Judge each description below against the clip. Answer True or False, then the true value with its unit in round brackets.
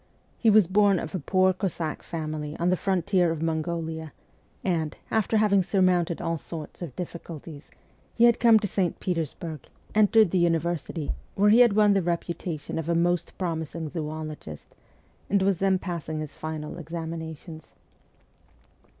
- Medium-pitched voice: True (170 Hz)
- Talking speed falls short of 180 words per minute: True (150 wpm)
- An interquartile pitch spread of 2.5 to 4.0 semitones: True (3.2 semitones)